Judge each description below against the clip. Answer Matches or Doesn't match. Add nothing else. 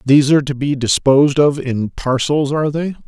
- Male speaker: Matches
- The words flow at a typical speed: Matches